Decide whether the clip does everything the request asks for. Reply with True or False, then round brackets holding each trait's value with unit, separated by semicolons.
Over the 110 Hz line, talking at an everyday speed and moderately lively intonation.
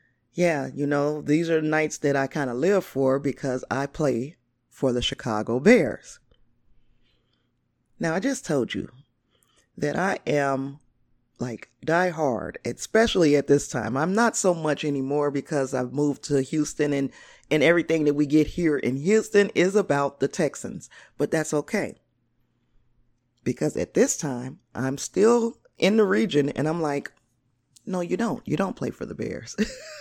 True (140 Hz; 160 wpm; 4.1 semitones)